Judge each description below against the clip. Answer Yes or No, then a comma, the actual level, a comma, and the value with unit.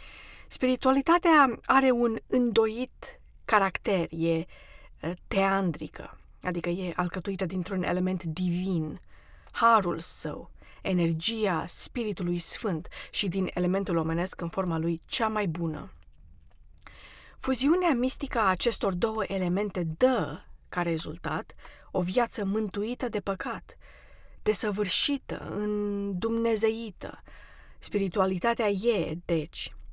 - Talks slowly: Yes, slow, 95 wpm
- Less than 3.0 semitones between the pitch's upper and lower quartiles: No, average, 4.5 semitones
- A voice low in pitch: No, high, 195 Hz